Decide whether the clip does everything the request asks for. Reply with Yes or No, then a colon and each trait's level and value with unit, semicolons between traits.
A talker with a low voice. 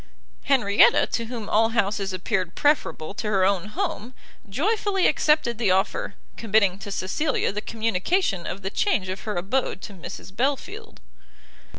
No: high, 215 Hz